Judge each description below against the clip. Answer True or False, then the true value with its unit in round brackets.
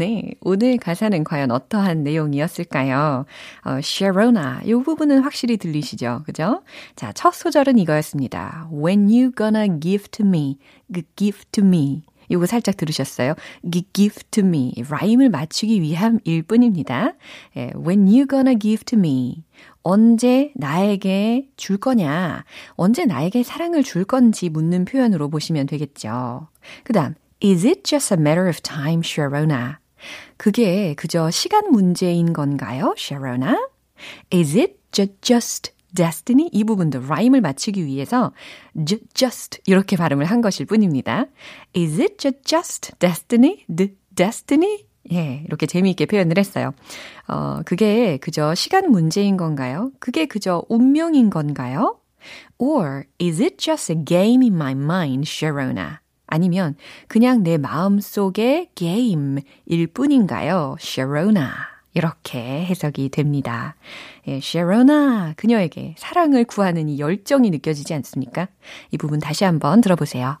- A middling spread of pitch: False (7.5 semitones)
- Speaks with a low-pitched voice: False (185 Hz)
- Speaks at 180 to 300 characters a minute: False (355 characters per minute)